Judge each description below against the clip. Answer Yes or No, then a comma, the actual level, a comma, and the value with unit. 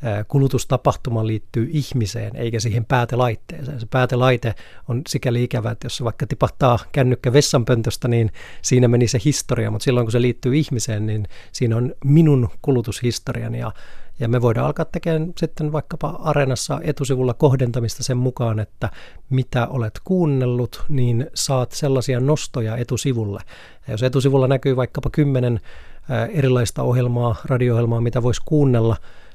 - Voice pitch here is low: Yes, low, 125 Hz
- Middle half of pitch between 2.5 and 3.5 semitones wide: Yes, average, 2.9 semitones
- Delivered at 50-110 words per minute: No, average, 135 wpm